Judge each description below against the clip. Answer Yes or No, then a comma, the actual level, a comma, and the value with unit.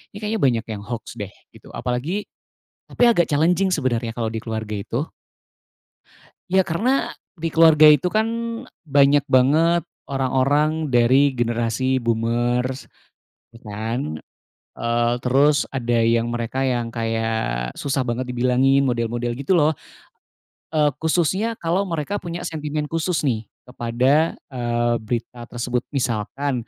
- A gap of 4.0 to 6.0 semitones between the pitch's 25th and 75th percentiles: Yes, average, 4.6 semitones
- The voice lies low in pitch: Yes, low, 130 Hz